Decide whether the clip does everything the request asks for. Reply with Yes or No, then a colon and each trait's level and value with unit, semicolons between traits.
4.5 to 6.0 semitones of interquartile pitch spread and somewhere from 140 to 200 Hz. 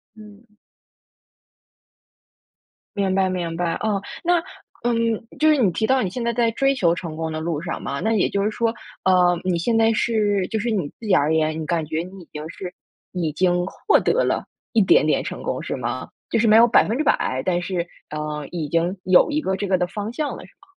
Yes: average, 5.0 semitones; high, 190 Hz